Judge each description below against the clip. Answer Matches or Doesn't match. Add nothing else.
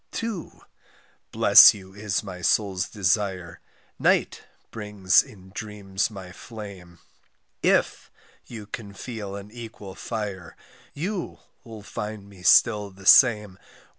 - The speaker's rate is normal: Doesn't match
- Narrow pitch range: Matches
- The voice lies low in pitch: Matches